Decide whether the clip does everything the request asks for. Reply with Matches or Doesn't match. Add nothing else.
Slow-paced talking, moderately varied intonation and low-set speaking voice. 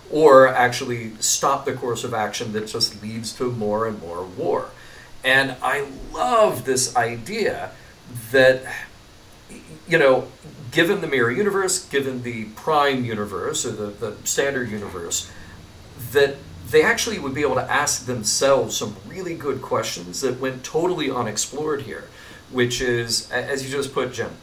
Doesn't match